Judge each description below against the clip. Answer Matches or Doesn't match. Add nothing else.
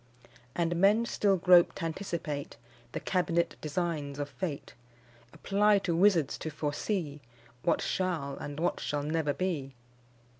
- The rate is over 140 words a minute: Doesn't match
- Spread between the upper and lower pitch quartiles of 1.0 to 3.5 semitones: Doesn't match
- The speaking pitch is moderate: Matches